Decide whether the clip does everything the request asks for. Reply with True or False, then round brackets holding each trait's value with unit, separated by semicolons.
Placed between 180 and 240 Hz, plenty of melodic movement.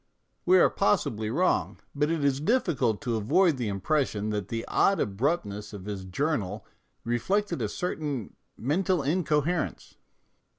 False (135 Hz; 7.8 semitones)